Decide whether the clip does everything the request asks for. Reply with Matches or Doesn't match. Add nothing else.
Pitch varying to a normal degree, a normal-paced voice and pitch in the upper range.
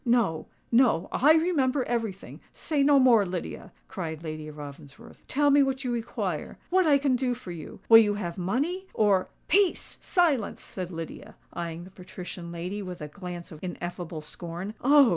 Doesn't match